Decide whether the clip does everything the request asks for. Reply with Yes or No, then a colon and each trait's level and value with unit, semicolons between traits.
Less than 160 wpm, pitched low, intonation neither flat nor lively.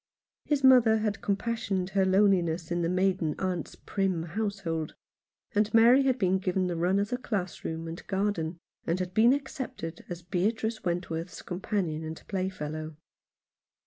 No: average, 145 wpm; medium, 185 Hz; average, 3.6 semitones